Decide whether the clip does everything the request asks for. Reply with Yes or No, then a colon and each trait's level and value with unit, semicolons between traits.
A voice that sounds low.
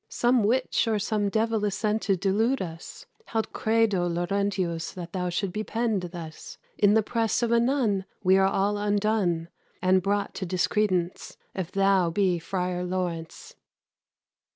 No: high, 195 Hz